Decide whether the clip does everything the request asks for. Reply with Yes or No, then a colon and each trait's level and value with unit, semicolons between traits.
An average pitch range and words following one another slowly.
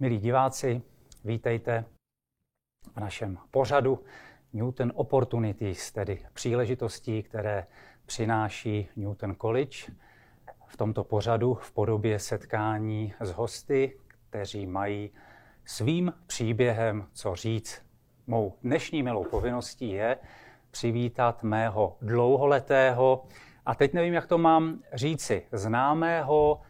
Yes: average, 3.3 semitones; slow, 100 wpm